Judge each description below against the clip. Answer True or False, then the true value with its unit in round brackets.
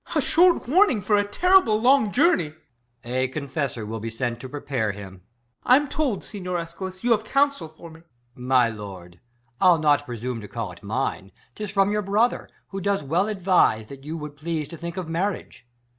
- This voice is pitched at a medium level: True (165 Hz)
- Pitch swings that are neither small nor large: False (8.7 semitones)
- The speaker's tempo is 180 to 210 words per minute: True (205 wpm)